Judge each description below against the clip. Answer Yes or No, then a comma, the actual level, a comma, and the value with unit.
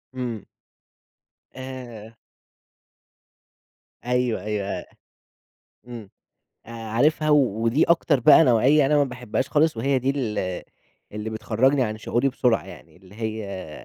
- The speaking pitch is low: Yes, low, 120 Hz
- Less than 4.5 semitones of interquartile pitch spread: Yes, average, 3.7 semitones